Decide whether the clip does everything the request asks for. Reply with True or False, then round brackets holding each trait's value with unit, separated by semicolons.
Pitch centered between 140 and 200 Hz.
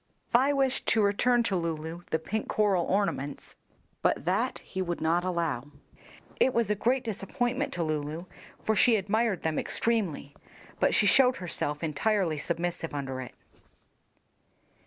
True (185 Hz)